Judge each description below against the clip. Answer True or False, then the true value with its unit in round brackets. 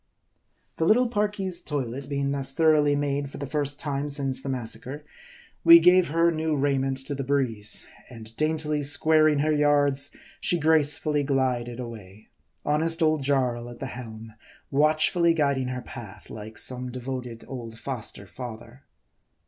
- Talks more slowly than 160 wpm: True (150 wpm)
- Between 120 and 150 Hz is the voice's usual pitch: True (140 Hz)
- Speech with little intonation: False (3.5 semitones)